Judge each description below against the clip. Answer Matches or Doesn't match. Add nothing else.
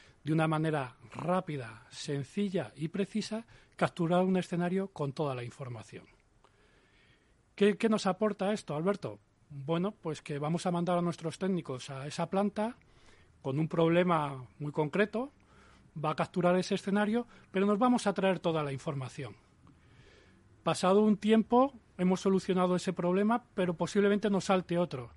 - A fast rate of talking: Doesn't match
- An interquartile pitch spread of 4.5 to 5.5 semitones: Matches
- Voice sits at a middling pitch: Matches